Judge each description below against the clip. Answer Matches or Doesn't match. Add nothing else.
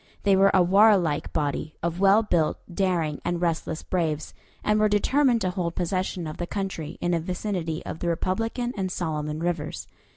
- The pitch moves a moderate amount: Matches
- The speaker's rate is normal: Matches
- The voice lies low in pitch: Doesn't match